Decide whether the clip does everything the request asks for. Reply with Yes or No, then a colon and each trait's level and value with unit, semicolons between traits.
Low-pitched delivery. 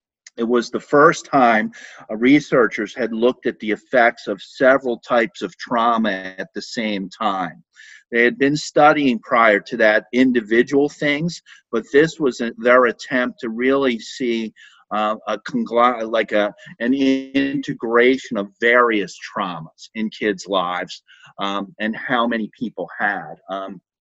Yes: low, 115 Hz